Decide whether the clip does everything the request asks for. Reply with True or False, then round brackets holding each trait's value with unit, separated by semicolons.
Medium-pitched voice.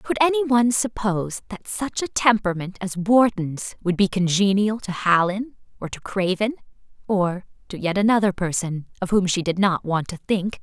False (200 Hz)